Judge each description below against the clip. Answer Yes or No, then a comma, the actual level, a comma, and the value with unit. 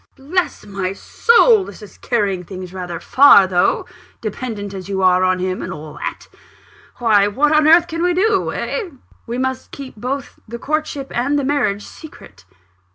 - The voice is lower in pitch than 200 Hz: No, high, 235 Hz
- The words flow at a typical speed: Yes, average, 170 wpm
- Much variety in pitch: Yes, wide, 7.5 semitones